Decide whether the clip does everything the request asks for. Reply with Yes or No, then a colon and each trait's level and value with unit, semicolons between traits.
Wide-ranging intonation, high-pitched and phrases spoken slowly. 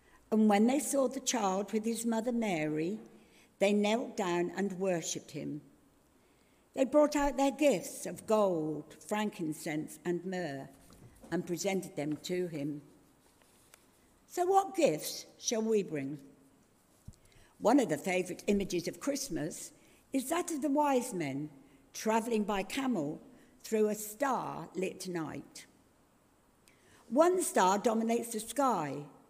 Yes: wide, 7.0 semitones; high, 205 Hz; slow, 130 wpm